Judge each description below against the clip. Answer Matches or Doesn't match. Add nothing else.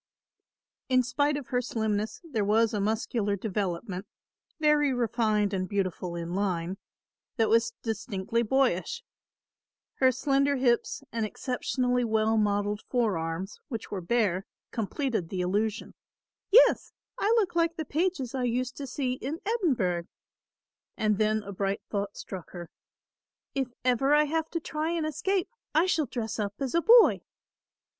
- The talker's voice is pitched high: Matches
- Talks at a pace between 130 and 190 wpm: Matches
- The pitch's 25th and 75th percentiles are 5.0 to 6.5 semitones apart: Matches